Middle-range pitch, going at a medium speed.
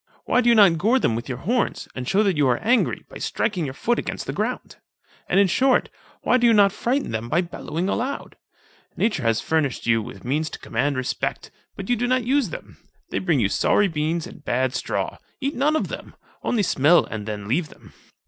No: medium, 175 Hz; fast, 220 wpm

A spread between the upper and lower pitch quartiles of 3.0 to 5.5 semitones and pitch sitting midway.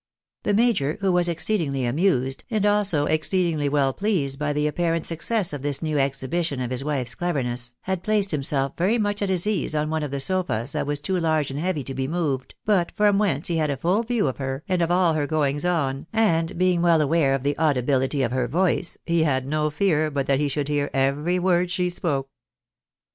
Yes: average, 4.5 semitones; medium, 155 Hz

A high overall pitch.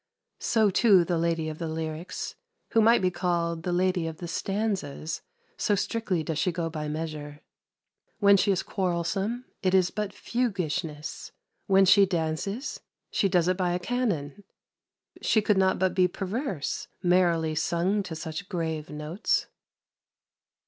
No: medium, 180 Hz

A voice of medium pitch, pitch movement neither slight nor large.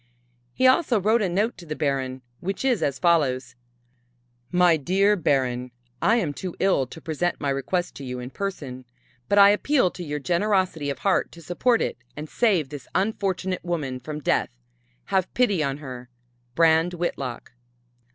No: medium, 170 Hz; wide, 5.9 semitones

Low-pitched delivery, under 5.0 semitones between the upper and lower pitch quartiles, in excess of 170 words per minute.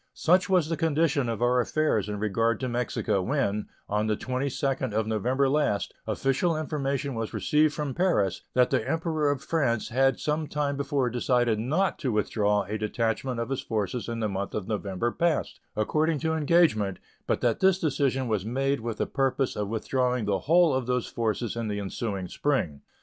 No: low, 125 Hz; average, 5.3 semitones; average, 185 wpm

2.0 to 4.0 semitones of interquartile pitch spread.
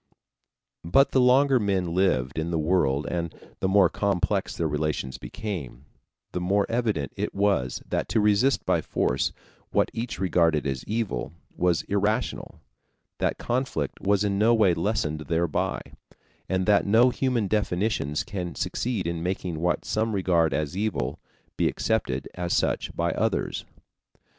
No: average, 4.8 semitones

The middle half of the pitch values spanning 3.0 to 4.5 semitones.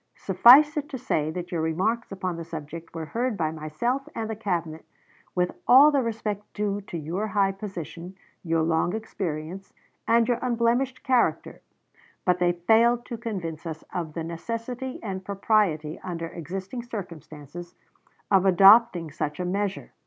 No: wide, 5.6 semitones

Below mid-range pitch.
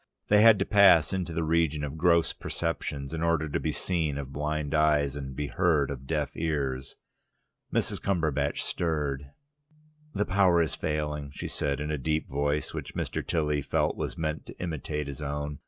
Yes: very low, 75 Hz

